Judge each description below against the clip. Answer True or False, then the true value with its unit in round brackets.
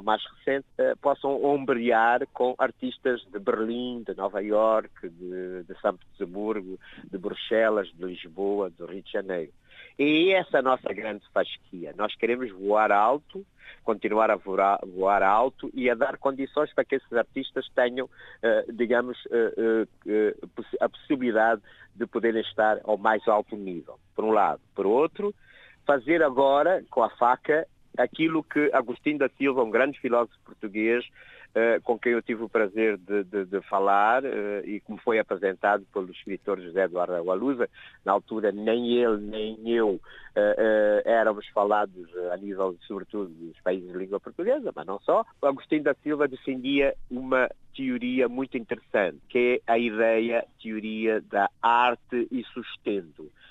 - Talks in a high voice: False (115 Hz)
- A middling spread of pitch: True (4.0 semitones)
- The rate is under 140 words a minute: False (155 wpm)